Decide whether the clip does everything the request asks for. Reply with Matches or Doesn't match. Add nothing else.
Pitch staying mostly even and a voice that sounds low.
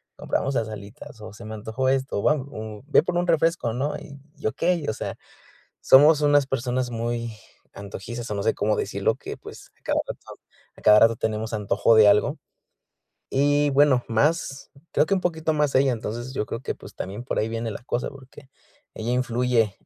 Doesn't match